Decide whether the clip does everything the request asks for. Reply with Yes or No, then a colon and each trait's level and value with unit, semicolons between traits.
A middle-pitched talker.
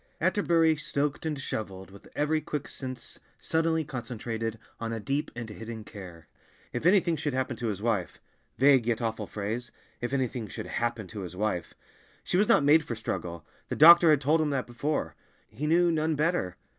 No: low, 130 Hz